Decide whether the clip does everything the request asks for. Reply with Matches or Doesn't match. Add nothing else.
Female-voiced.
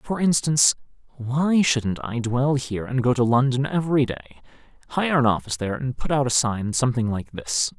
Doesn't match